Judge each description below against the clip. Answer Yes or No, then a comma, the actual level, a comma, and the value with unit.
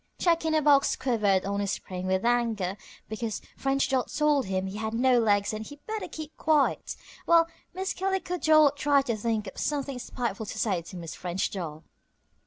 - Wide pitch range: Yes, wide, 6.6 semitones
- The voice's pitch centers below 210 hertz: No, high, 235 Hz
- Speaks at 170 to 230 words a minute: Yes, average, 195 wpm